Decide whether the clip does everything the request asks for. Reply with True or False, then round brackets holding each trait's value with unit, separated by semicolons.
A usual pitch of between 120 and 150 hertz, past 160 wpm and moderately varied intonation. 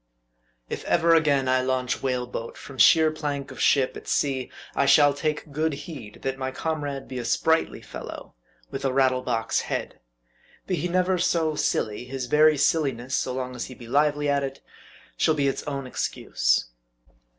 True (140 Hz; 180 wpm; 3.1 semitones)